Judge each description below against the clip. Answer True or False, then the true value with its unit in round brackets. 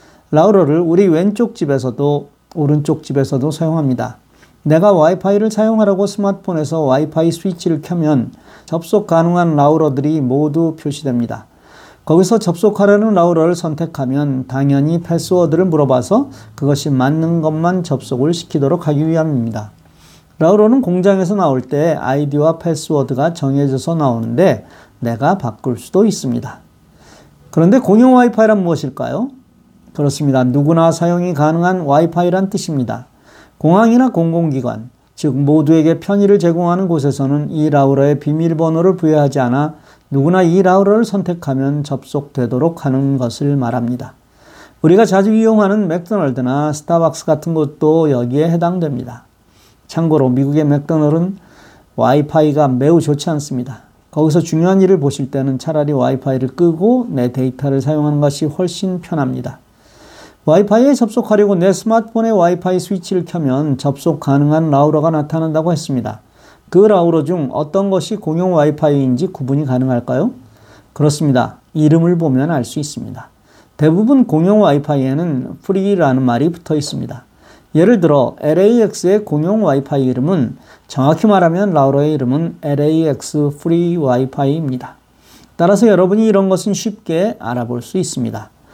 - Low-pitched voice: False (155 Hz)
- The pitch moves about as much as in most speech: True (4.5 semitones)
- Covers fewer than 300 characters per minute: False (355 characters per minute)